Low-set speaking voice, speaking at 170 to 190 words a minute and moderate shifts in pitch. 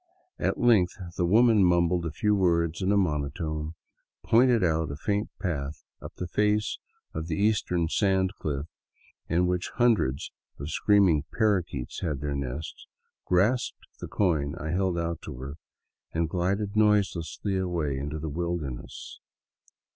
No: very low, 85 Hz; average, 145 wpm; average, 4.5 semitones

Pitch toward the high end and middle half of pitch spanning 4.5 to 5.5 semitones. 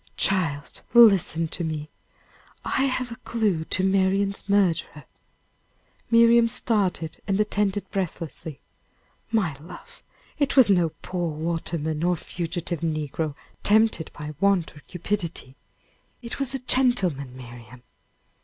No: medium, 180 Hz; average, 4.9 semitones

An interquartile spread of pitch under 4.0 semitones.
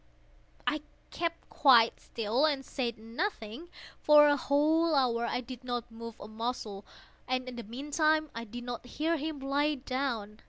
No: average, 4.3 semitones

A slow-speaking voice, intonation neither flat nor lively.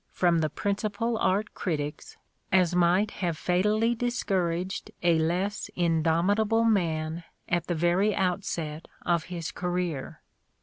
Yes: slow, 120 wpm; average, 3.3 semitones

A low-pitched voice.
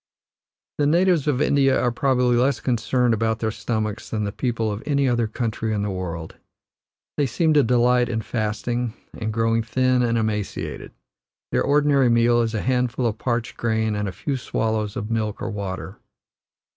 Yes: low, 115 Hz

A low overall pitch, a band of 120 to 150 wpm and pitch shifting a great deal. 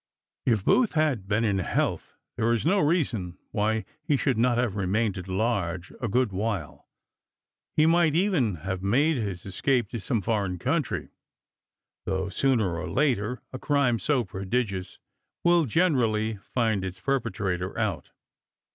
Yes: low, 110 Hz; average, 145 wpm; wide, 5.7 semitones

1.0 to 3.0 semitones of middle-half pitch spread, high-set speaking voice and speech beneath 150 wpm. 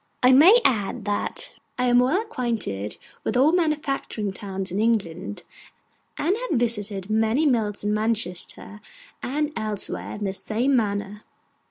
No: average, 4.2 semitones; high, 220 Hz; average, 140 wpm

